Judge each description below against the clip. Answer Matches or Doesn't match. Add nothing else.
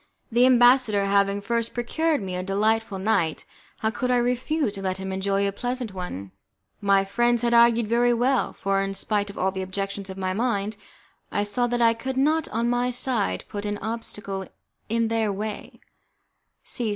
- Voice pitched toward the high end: Matches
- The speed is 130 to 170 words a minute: Doesn't match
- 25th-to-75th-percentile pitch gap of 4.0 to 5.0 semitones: Doesn't match